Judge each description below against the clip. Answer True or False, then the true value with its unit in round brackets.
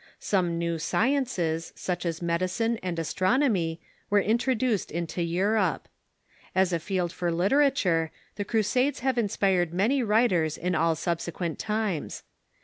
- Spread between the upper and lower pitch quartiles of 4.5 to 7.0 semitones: True (4.8 semitones)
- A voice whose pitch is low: False (185 Hz)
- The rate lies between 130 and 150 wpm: True (135 wpm)